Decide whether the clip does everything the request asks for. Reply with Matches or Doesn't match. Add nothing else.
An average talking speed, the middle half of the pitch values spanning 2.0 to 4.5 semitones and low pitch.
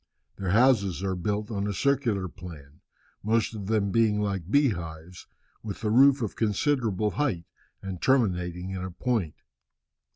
Matches